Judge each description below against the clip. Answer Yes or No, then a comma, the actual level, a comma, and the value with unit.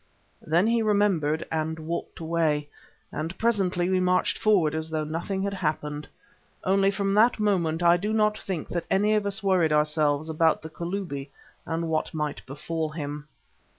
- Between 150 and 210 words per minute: Yes, average, 165 wpm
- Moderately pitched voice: Yes, medium, 170 Hz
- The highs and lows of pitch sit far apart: No, average, 4.0 semitones